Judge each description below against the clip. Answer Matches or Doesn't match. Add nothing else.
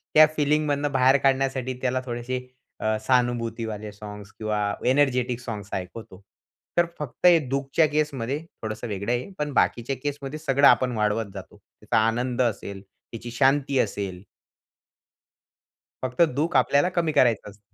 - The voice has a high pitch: Doesn't match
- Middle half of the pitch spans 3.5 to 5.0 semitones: Matches